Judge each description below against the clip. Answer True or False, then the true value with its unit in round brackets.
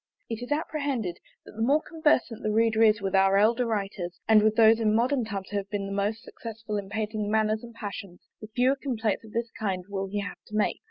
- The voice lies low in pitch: False (215 Hz)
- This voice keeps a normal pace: False (230 wpm)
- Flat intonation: True (2.3 semitones)